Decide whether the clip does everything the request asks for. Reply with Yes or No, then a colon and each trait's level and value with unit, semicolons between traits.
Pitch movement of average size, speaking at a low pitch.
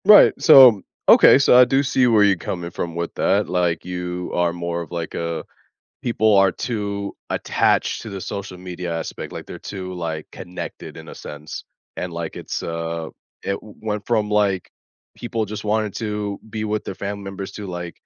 Yes: average, 3.5 semitones; very low, 95 Hz